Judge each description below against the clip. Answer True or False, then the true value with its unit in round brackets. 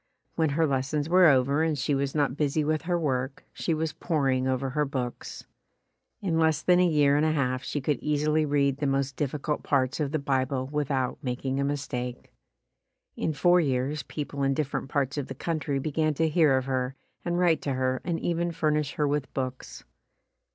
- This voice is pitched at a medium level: True (145 Hz)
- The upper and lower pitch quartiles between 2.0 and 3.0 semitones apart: True (2.6 semitones)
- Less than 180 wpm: False (200 wpm)